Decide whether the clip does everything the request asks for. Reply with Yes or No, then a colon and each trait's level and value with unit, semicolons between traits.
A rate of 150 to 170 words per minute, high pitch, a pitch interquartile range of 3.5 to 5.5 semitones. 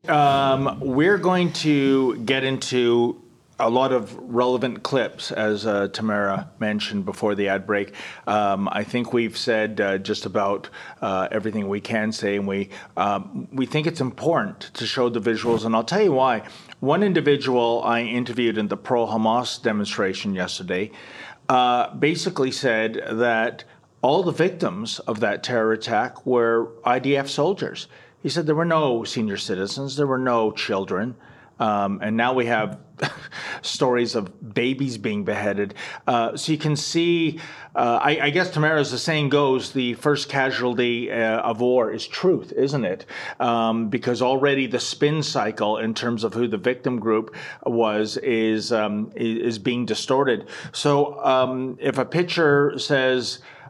No: average, 160 wpm; low, 125 Hz; average, 3.9 semitones